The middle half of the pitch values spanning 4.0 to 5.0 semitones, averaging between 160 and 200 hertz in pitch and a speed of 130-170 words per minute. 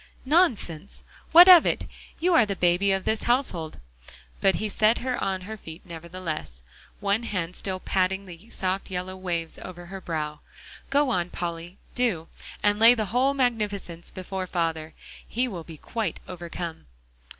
Yes: average, 4.4 semitones; high, 190 Hz; average, 160 wpm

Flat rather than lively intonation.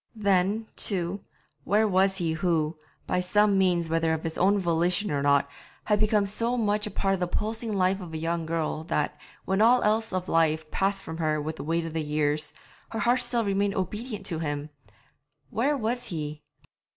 No: average, 4.5 semitones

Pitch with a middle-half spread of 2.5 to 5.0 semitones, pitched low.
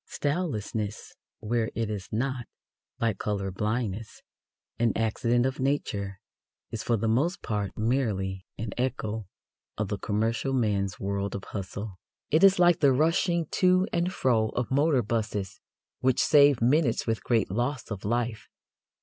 Yes: average, 4.3 semitones; low, 115 Hz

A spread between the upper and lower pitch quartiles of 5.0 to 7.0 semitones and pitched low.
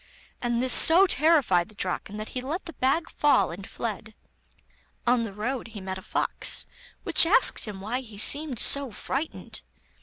No: average, 5.3 semitones; high, 240 Hz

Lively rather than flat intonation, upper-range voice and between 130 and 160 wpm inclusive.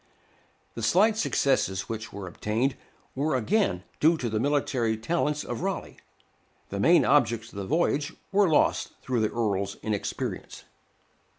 No: wide, 6.3 semitones; low, 120 Hz; average, 140 wpm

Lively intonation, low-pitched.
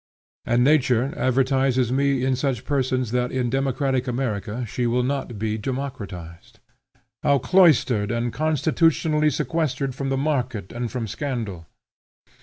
No: narrow, 2.6 semitones; low, 130 Hz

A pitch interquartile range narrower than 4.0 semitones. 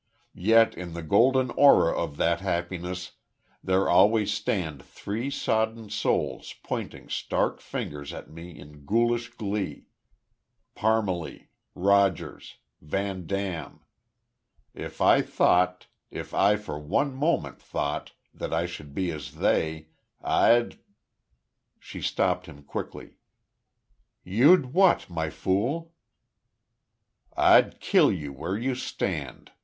No: wide, 5.5 semitones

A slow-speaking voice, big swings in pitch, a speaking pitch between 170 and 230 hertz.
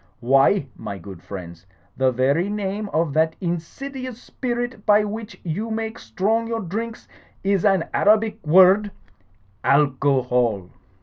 Yes: slow, 125 wpm; wide, 8.2 semitones; high, 190 Hz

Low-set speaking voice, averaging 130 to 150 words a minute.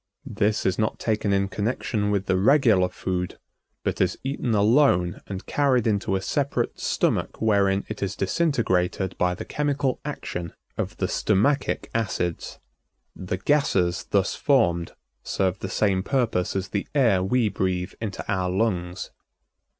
Yes: low, 100 Hz; average, 145 wpm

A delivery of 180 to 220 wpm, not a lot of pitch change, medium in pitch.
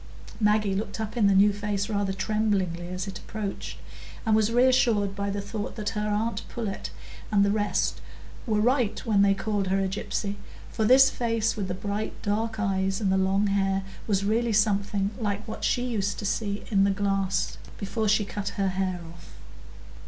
No: average, 190 wpm; narrow, 1.8 semitones; high, 205 Hz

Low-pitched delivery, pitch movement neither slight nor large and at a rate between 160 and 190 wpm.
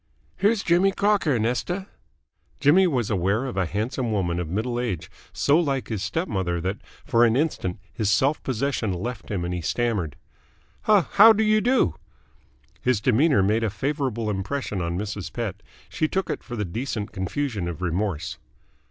No: low, 115 Hz; wide, 6.8 semitones; average, 170 wpm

